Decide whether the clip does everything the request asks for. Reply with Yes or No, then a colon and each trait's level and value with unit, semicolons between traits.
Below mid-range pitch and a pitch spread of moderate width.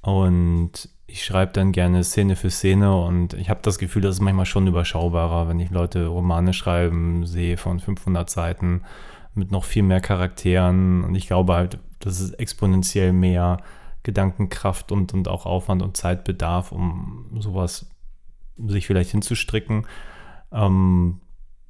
No: very low, 95 Hz; narrow, 1.7 semitones